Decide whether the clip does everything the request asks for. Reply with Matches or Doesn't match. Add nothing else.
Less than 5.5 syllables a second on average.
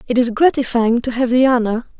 Doesn't match